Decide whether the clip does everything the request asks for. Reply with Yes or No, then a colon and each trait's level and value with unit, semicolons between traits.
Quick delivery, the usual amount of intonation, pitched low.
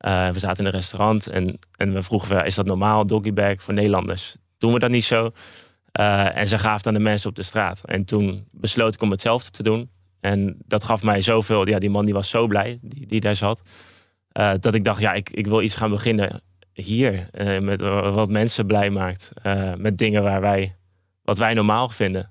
No: fast, 225 wpm; narrow, 2.1 semitones; low, 105 Hz